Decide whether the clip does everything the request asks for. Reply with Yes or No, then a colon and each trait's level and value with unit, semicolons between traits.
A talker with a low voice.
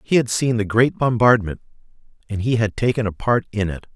Yes: low, 110 Hz